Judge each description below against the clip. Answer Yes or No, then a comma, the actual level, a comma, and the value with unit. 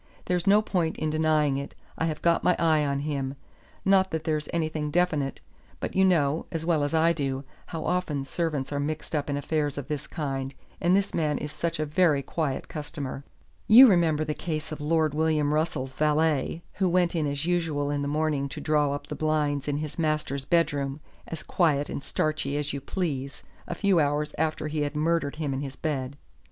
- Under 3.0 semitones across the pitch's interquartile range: Yes, narrow, 2.4 semitones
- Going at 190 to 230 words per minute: Yes, fast, 205 wpm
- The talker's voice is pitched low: No, medium, 155 Hz